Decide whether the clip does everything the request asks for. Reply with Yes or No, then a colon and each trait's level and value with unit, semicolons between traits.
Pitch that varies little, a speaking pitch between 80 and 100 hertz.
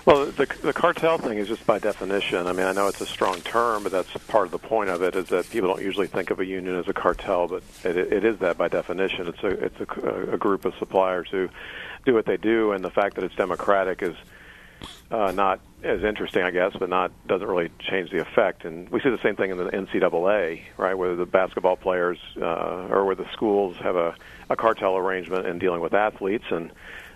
Yes: narrow, 1.6 semitones; very low, 95 Hz